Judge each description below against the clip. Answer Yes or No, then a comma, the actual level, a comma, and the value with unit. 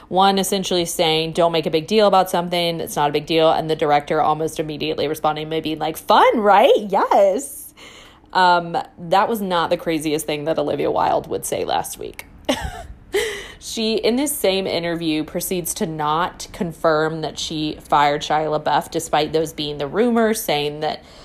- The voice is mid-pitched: Yes, medium, 165 Hz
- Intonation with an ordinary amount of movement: Yes, average, 3.8 semitones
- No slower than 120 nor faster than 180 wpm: Yes, average, 170 wpm